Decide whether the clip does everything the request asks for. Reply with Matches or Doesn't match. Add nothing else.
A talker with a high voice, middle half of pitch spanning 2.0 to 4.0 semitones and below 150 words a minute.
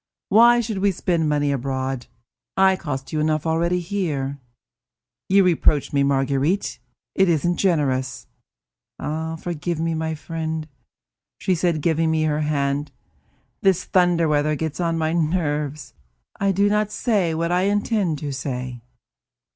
Doesn't match